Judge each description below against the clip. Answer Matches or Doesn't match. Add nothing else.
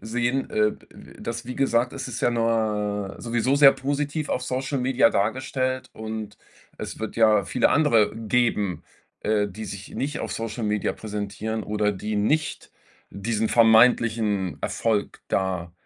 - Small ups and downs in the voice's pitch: Doesn't match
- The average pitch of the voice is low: Matches